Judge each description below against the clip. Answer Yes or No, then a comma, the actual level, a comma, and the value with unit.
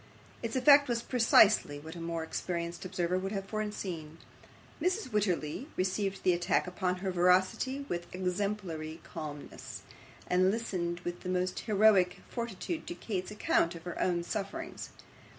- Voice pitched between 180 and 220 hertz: Yes, medium, 185 Hz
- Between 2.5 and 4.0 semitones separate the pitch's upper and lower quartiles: Yes, average, 3.7 semitones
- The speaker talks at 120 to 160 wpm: Yes, average, 145 wpm